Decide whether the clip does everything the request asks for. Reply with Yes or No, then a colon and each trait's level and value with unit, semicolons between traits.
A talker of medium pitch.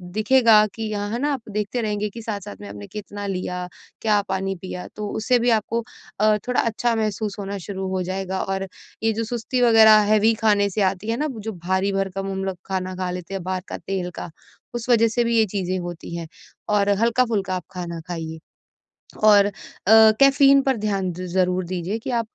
No: high, 205 Hz